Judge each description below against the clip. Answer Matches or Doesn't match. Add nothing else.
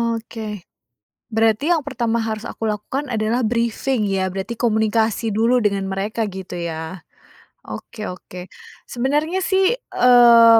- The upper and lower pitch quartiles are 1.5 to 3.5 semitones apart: Matches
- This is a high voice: Matches